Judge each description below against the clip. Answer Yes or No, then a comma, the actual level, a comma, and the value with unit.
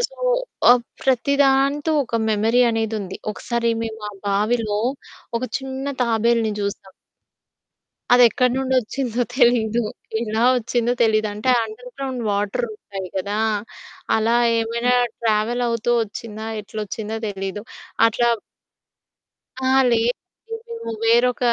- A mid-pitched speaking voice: No, high, 230 Hz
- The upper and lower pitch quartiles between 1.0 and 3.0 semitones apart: Yes, narrow, 2.6 semitones